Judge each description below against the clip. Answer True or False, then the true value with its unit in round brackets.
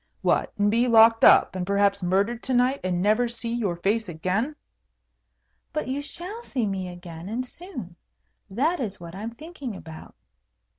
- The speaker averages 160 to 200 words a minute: True (170 wpm)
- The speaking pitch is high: True (220 Hz)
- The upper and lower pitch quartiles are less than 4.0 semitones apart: False (5.2 semitones)